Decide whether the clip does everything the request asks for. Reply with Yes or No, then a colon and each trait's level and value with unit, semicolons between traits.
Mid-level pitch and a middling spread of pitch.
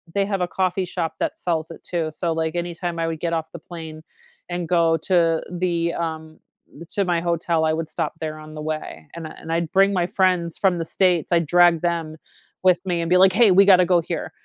No: medium, 170 Hz; narrow, 1.9 semitones